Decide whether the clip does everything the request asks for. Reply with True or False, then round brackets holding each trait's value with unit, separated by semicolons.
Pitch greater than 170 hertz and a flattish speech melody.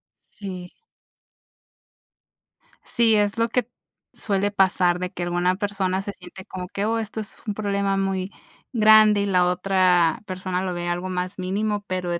True (190 Hz; 2.2 semitones)